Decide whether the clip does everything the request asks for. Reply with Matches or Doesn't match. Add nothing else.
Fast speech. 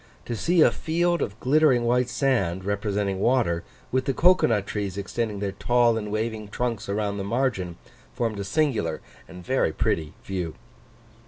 Doesn't match